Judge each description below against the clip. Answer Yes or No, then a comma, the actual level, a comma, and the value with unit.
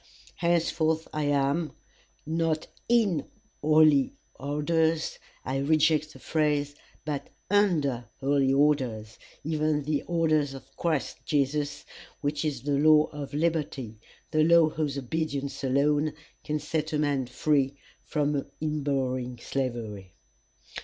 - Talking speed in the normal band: No, slow, 120 wpm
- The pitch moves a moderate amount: No, narrow, 2.2 semitones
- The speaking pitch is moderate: Yes, medium, 150 Hz